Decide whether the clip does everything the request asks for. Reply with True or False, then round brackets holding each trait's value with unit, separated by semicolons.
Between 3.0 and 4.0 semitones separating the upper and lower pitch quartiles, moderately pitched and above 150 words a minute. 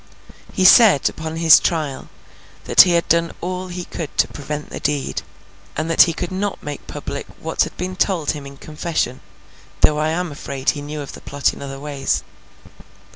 True (3.5 semitones; 155 Hz; 185 wpm)